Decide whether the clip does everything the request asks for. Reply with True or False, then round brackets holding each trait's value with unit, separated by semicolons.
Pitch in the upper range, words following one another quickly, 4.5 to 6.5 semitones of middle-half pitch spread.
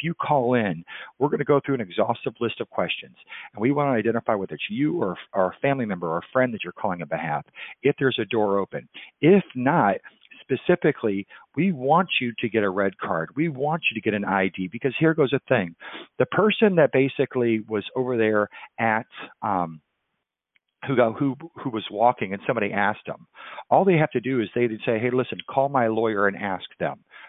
False (120 Hz; 210 wpm; 5.1 semitones)